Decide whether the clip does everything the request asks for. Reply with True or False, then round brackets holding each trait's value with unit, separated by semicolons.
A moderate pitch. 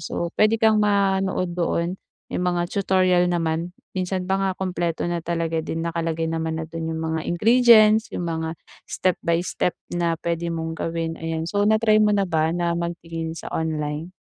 True (170 Hz)